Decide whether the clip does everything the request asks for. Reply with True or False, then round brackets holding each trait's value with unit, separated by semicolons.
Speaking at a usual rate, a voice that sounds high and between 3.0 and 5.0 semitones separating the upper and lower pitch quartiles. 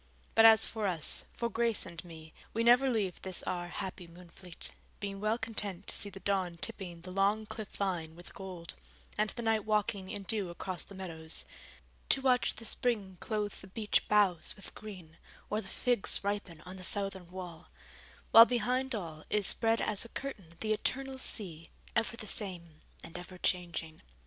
True (180 wpm; 195 Hz; 3.8 semitones)